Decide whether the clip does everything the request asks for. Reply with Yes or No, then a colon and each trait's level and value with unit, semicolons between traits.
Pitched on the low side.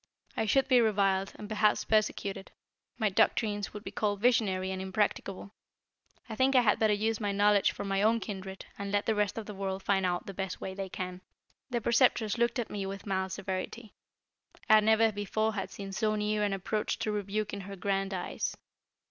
No: high, 205 Hz